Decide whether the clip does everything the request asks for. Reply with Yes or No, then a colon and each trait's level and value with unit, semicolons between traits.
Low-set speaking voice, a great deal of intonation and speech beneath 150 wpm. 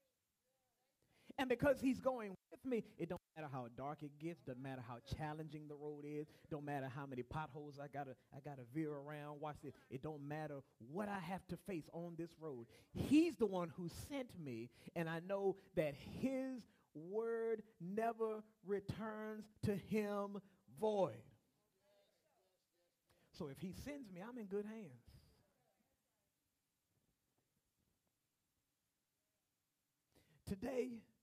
No: medium, 170 Hz; wide, 6.8 semitones; slow, 135 wpm